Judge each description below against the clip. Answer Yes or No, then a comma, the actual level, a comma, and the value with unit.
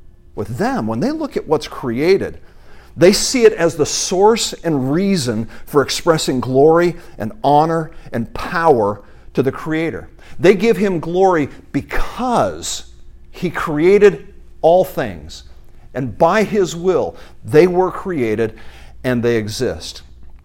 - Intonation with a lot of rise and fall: Yes, wide, 8.1 semitones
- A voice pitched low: No, medium, 160 Hz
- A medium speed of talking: No, slow, 130 wpm